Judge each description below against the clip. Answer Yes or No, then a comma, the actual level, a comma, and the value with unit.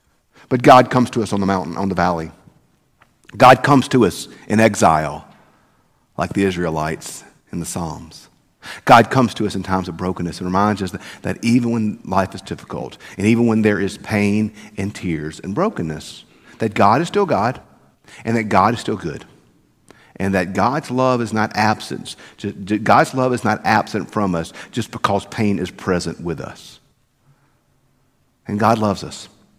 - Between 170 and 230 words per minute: Yes, average, 180 wpm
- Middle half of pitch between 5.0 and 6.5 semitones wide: No, average, 4.1 semitones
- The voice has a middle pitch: No, low, 105 Hz